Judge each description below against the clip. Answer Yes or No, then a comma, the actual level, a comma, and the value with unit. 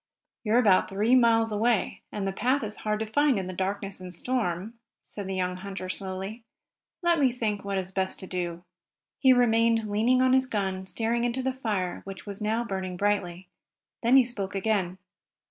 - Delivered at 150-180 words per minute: No, average, 190 wpm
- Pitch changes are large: No, average, 3.8 semitones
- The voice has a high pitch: Yes, high, 210 Hz